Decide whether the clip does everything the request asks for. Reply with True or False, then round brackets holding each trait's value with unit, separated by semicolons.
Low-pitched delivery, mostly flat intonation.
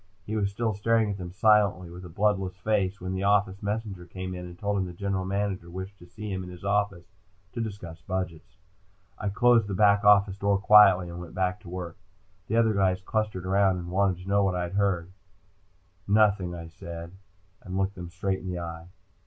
True (95 Hz; 2.2 semitones)